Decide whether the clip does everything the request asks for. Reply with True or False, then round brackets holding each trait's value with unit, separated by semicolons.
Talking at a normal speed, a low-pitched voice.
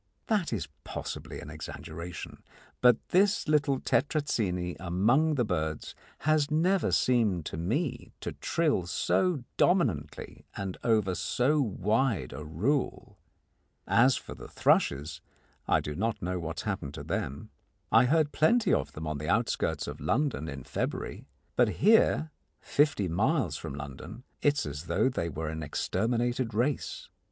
True (145 wpm; 110 Hz)